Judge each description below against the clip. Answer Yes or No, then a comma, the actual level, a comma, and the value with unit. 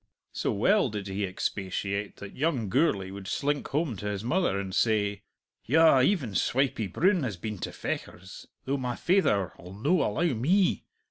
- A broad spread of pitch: Yes, wide, 6.9 semitones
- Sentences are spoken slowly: No, average, 165 wpm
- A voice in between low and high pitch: No, low, 110 Hz